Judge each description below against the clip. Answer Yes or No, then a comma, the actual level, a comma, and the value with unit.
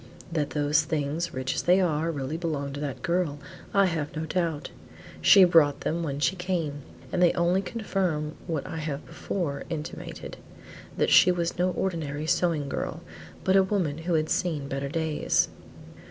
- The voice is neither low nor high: Yes, medium, 160 Hz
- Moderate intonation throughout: Yes, average, 3.3 semitones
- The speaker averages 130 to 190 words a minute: Yes, average, 170 wpm